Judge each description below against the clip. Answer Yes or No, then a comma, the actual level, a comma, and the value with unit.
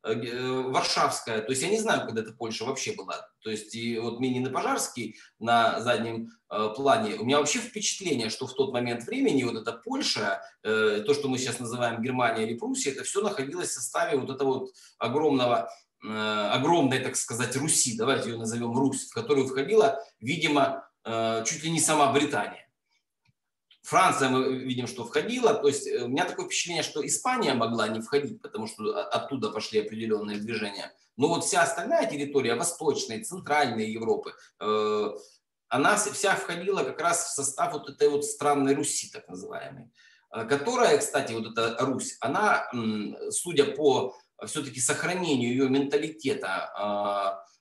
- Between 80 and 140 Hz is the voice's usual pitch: Yes, low, 135 Hz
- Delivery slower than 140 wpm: No, average, 155 wpm